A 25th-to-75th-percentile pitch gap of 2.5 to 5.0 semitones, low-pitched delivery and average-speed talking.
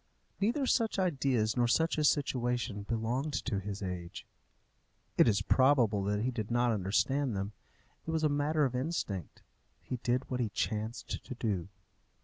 No: wide, 5.4 semitones; low, 120 Hz; average, 160 wpm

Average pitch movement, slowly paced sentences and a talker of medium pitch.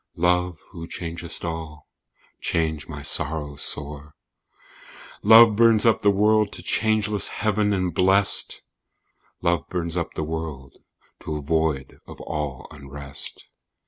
No: average, 5.0 semitones; slow, 125 wpm; very low, 85 Hz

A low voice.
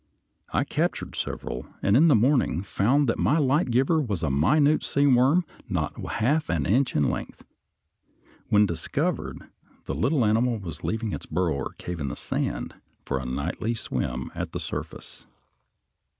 Yes: low, 110 Hz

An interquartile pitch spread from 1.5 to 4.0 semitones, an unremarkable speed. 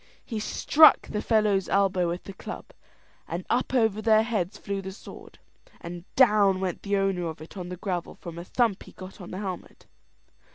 Yes: average, 3.0 semitones; average, 195 wpm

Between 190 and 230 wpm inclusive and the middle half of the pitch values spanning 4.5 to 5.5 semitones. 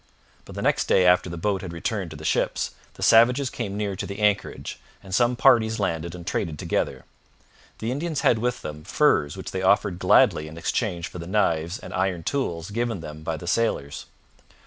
Yes: average, 200 wpm; average, 5.1 semitones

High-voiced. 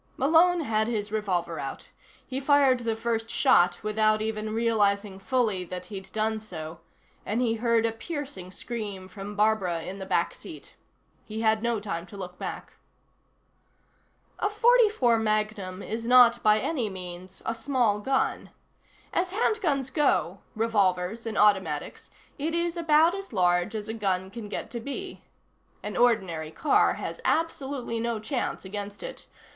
Yes: high, 220 Hz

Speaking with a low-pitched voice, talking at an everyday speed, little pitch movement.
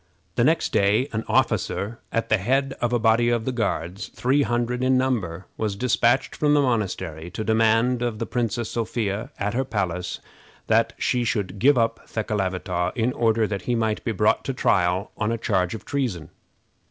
No: low, 115 Hz; average, 185 wpm; average, 3.4 semitones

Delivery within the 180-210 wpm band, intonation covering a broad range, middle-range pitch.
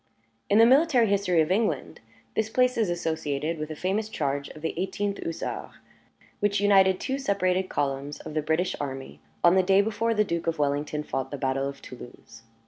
Yes: average, 190 wpm; wide, 5.7 semitones; medium, 175 Hz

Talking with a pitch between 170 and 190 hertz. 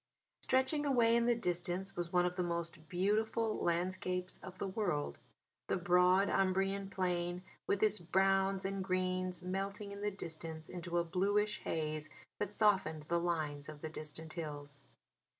Yes: medium, 185 Hz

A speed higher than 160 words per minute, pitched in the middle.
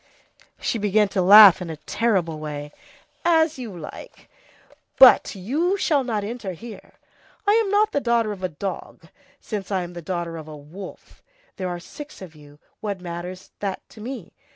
No: average, 170 wpm; high, 195 Hz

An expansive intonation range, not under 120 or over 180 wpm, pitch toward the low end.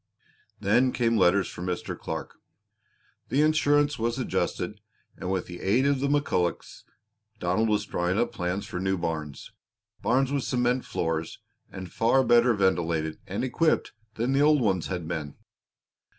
Yes: wide, 6.6 semitones; average, 150 wpm; low, 105 Hz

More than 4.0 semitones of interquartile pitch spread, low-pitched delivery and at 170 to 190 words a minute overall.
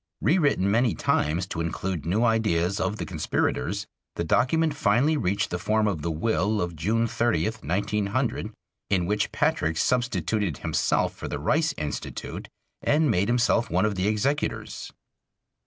No: average, 5.3 semitones; low, 105 Hz; average, 150 wpm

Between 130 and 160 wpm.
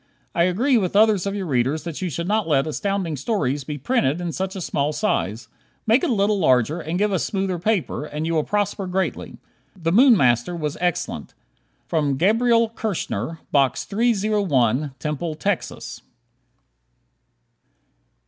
Yes: average, 155 wpm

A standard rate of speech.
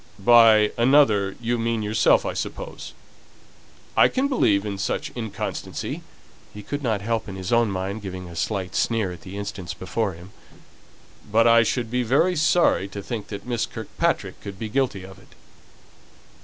Yes: average, 170 wpm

